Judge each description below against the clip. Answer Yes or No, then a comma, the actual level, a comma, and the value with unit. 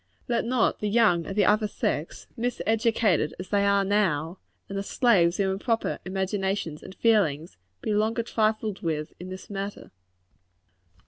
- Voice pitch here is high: Yes, high, 200 Hz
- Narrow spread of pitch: No, average, 3.1 semitones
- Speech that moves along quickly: No, average, 150 wpm